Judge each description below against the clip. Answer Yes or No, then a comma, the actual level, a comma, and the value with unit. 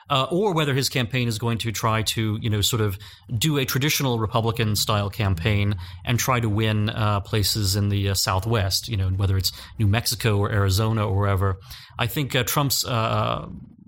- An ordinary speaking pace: Yes, average, 195 wpm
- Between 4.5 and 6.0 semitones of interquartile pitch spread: No, average, 3.0 semitones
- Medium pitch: No, low, 110 Hz